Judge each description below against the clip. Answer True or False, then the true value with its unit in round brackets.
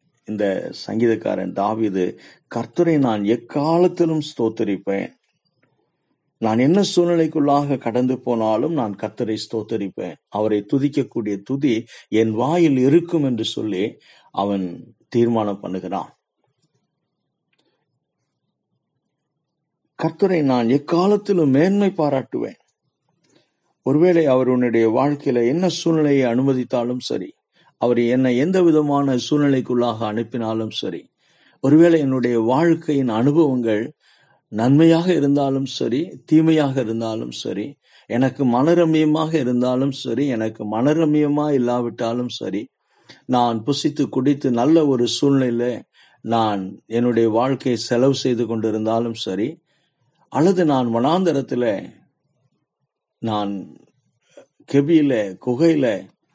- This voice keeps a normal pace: True (90 wpm)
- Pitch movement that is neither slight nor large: True (4.6 semitones)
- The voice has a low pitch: True (130 Hz)